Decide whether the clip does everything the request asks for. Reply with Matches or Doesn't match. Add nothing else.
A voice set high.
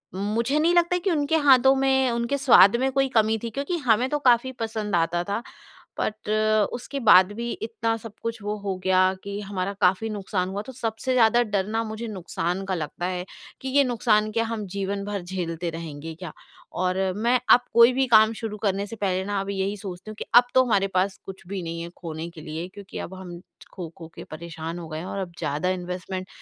Matches